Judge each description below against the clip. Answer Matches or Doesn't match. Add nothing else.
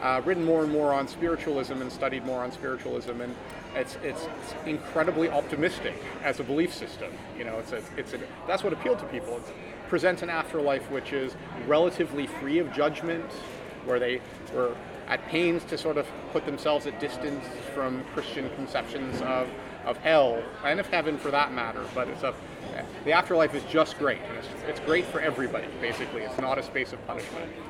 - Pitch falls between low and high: Matches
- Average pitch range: Matches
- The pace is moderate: Matches